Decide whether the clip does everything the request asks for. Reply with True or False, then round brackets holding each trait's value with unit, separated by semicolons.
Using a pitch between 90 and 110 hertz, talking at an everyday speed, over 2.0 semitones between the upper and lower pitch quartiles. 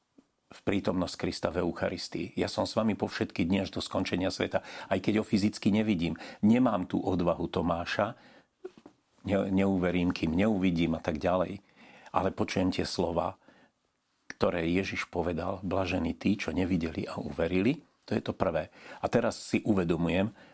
True (95 Hz; 155 wpm; 2.4 semitones)